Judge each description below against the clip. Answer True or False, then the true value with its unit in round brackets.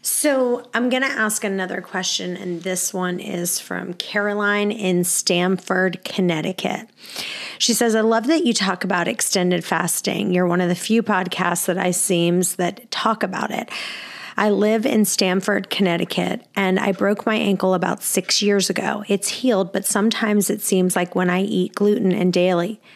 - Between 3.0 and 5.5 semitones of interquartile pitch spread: False (2.6 semitones)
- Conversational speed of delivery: True (175 wpm)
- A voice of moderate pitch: False (195 Hz)